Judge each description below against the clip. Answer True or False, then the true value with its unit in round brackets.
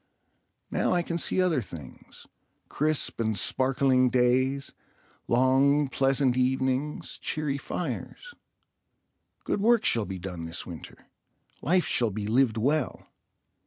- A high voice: False (130 Hz)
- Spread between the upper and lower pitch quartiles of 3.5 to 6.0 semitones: True (4.1 semitones)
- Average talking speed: False (115 wpm)